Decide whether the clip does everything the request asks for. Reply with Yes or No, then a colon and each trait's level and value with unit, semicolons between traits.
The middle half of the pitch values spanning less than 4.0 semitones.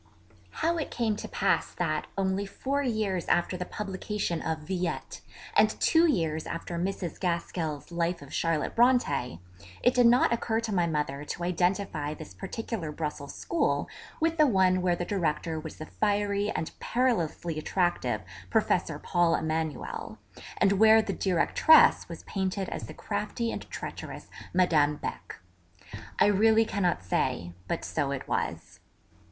No: average, 5.1 semitones